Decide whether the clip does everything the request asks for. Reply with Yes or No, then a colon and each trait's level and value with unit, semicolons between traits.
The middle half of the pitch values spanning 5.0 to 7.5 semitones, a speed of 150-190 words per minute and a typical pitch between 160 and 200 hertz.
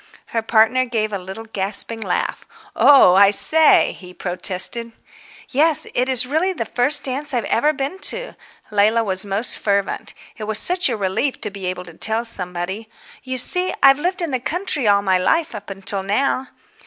No: wide, 5.4 semitones; average, 180 wpm; high, 225 Hz